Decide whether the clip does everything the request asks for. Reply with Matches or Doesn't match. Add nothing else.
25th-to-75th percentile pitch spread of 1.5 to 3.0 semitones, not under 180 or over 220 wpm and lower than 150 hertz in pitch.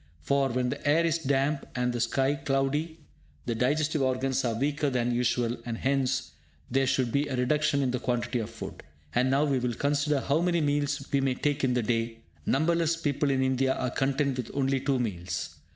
Matches